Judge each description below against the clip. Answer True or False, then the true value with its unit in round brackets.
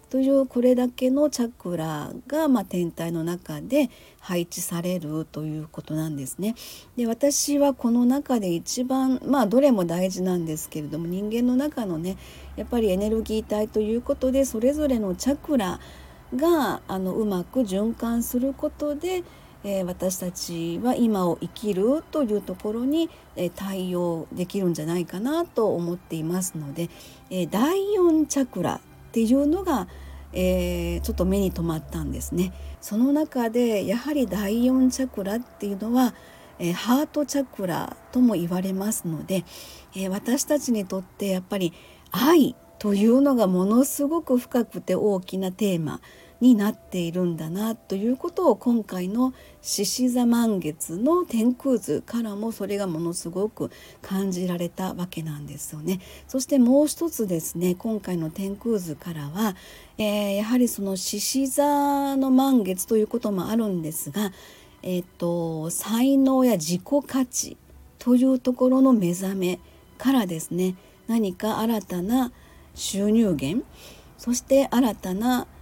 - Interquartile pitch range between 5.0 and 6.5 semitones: True (6.2 semitones)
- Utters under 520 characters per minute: True (300 characters per minute)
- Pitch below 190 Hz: False (210 Hz)